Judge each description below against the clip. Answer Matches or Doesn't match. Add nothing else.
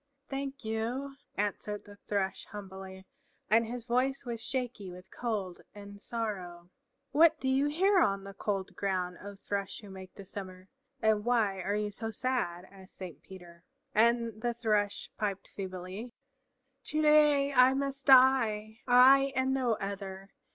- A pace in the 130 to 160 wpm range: Matches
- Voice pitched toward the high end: Matches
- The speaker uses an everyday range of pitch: Matches